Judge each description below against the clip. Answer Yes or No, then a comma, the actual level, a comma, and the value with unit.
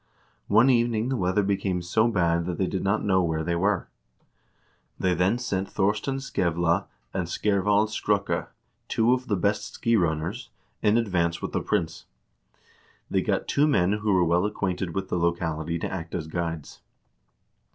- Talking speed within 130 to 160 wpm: No, average, 170 wpm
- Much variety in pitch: No, average, 3.6 semitones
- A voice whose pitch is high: No, very low, 95 Hz